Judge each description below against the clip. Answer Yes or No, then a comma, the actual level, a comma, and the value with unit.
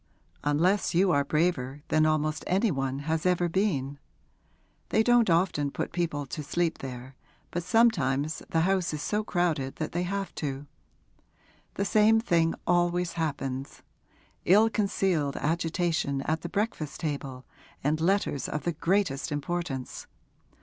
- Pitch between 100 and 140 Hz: No, medium, 165 Hz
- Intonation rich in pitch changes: No, average, 4.2 semitones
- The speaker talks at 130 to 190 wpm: Yes, average, 140 wpm